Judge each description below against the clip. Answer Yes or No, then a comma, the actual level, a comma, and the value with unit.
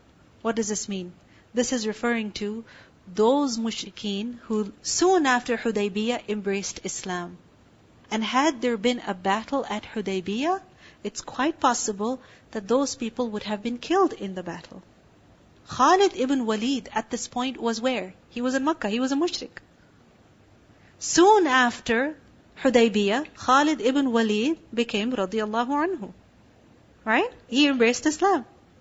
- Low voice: No, high, 235 Hz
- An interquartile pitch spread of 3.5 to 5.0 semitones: Yes, average, 4.1 semitones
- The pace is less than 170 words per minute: Yes, slow, 135 wpm